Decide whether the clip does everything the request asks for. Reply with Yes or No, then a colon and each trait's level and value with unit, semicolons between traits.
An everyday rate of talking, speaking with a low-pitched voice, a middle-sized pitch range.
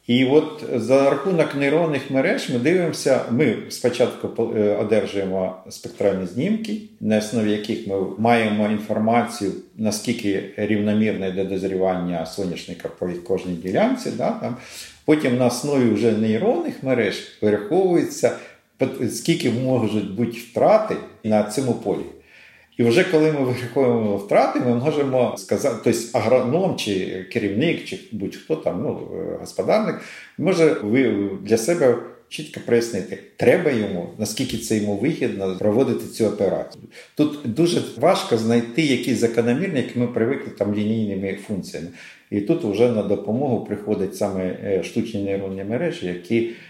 Yes: average, 125 wpm; low, 115 Hz; average, 3.8 semitones